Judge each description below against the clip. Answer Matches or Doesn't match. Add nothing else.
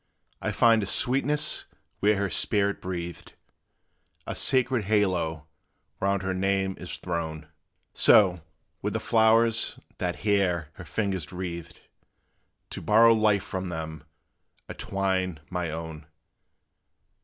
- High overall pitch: Doesn't match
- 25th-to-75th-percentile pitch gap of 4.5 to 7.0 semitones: Doesn't match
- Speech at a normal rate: Doesn't match